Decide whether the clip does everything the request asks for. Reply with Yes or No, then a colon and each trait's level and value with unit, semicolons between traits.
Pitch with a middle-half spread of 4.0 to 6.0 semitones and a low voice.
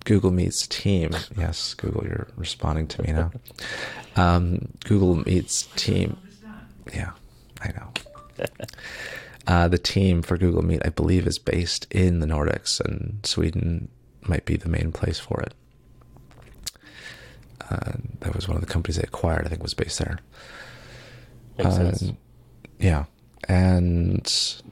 Yes: average, 4.4 semitones; very low, 95 Hz